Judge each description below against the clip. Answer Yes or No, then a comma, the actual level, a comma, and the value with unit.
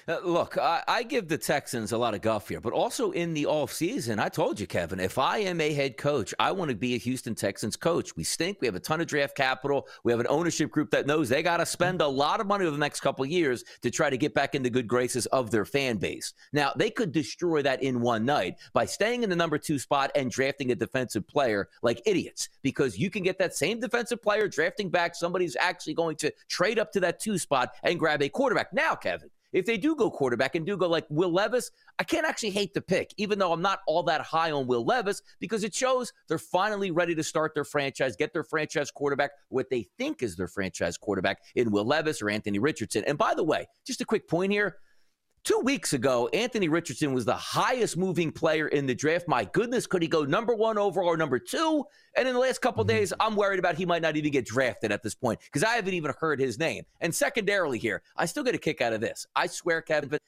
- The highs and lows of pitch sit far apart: Yes, wide, 6.7 semitones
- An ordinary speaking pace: No, fast, 255 wpm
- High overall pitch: No, medium, 160 Hz